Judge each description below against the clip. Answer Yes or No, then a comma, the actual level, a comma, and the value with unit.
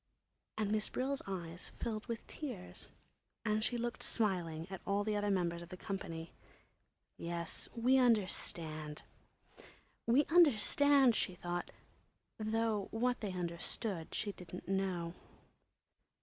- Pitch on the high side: Yes, high, 200 Hz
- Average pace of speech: No, slow, 120 wpm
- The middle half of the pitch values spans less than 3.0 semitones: No, average, 4.9 semitones